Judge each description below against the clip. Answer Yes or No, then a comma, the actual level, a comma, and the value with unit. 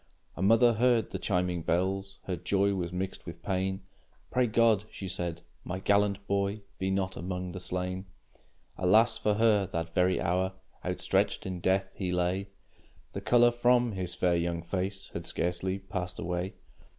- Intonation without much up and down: Yes, narrow, 2.0 semitones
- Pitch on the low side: Yes, very low, 95 Hz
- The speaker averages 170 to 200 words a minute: No, average, 160 wpm